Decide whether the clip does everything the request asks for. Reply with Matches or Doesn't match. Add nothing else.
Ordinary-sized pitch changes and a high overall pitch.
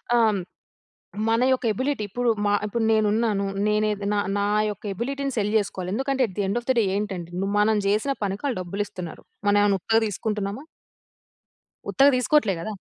Matches